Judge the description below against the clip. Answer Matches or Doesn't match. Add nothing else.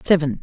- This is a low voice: Doesn't match